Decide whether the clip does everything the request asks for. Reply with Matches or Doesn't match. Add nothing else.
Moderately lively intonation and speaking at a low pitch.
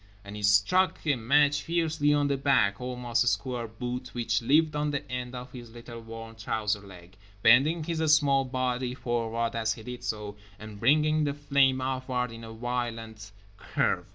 Matches